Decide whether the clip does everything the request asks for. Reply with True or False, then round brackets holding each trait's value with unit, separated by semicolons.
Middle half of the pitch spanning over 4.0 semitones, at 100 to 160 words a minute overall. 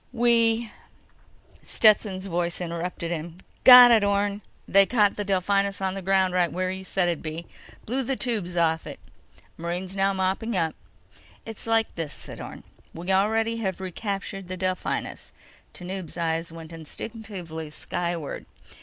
False (3.3 semitones; 145 wpm)